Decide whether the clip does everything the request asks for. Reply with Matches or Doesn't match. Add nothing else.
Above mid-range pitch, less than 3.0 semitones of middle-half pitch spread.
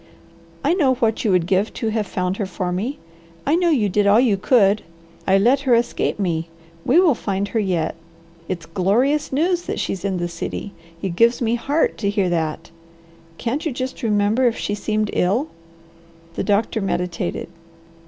Doesn't match